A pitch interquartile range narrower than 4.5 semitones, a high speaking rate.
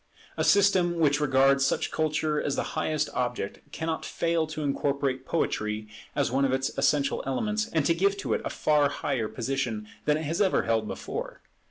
No: average, 3.2 semitones; average, 185 wpm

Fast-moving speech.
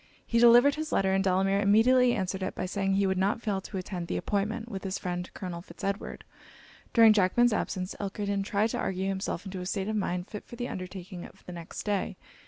Yes: fast, 220 wpm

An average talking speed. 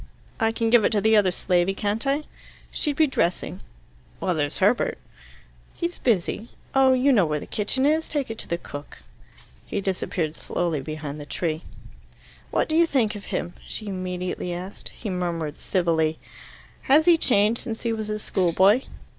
Yes: average, 175 wpm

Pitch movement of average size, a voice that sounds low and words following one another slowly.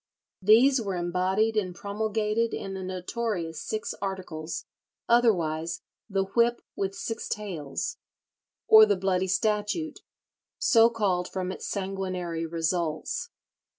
No: average, 3.4 semitones; high, 195 Hz; slow, 115 wpm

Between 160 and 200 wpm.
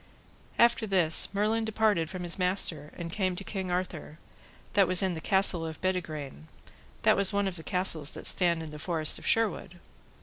Yes: average, 190 wpm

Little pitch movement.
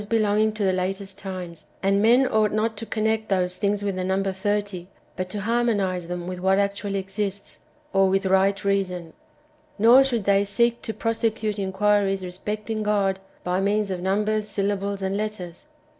Yes: narrow, 2.0 semitones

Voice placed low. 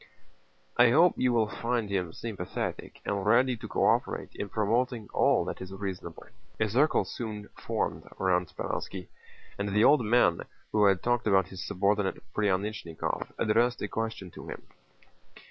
Yes: low, 105 Hz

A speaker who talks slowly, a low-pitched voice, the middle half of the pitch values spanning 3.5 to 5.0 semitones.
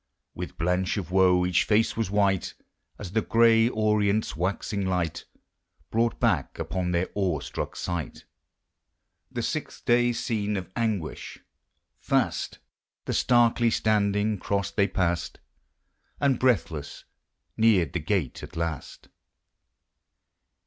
Yes: slow, 120 wpm; low, 100 Hz; average, 3.8 semitones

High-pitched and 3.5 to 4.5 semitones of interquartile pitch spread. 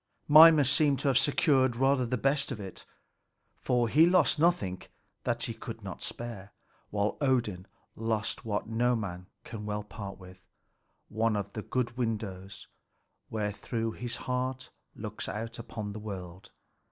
No: low, 115 Hz; average, 4.0 semitones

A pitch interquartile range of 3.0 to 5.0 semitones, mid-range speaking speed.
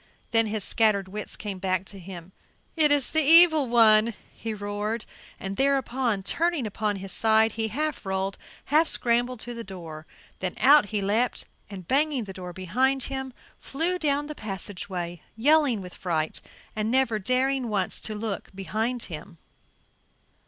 No: wide, 5.4 semitones; average, 160 wpm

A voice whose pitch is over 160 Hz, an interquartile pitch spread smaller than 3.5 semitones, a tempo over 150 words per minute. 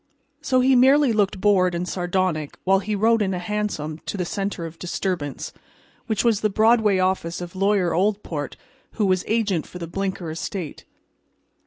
Yes: high, 190 Hz; average, 3.1 semitones; average, 170 wpm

